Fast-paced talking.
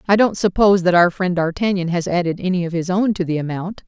Yes: fast, 250 wpm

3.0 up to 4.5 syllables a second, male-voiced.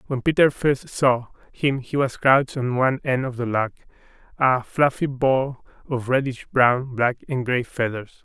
Yes: 4.4 syllables/s; male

